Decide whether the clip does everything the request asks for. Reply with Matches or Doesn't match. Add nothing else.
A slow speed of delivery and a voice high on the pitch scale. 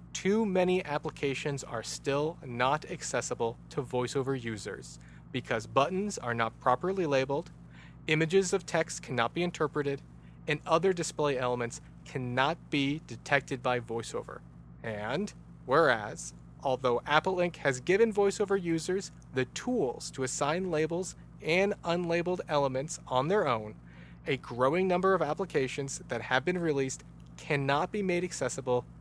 Doesn't match